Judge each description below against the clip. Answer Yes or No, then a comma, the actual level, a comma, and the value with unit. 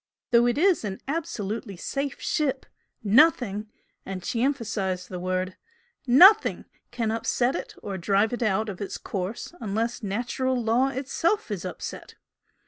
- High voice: Yes, high, 230 Hz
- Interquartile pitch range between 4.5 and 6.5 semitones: Yes, average, 5.0 semitones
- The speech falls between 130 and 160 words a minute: Yes, average, 140 wpm